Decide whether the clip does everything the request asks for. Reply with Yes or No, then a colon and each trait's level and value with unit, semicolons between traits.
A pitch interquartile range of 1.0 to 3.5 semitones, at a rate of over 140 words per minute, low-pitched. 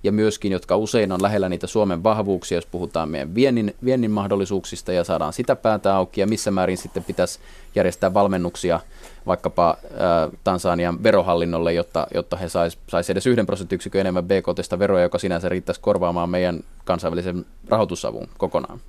Yes: average, 2.7 semitones; fast, 155 wpm; very low, 95 Hz